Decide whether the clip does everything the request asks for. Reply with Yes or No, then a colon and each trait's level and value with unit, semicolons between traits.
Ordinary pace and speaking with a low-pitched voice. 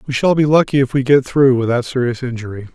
No: fast, 240 wpm; low, 130 Hz